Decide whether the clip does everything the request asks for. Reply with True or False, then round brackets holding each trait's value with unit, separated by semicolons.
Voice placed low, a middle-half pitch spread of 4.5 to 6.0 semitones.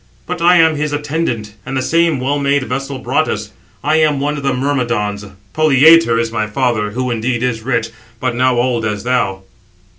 False (130 Hz; 4.0 semitones)